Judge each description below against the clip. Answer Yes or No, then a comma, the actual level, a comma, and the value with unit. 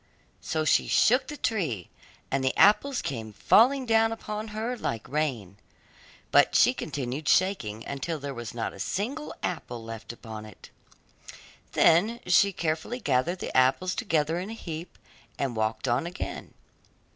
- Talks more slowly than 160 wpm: Yes, average, 150 wpm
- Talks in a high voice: No, medium, 160 Hz